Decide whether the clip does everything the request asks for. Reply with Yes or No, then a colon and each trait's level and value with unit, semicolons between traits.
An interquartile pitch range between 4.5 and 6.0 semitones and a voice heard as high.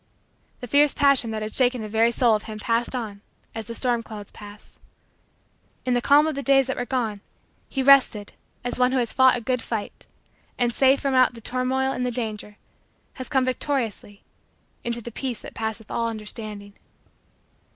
No: average, 3.0 semitones; high, 240 Hz